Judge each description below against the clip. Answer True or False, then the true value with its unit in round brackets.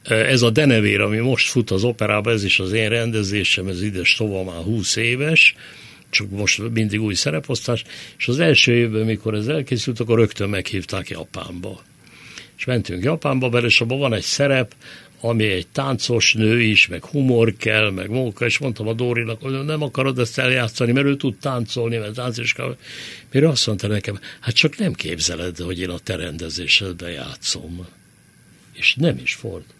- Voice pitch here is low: True (115 Hz)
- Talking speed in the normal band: False (180 wpm)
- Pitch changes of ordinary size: True (4.1 semitones)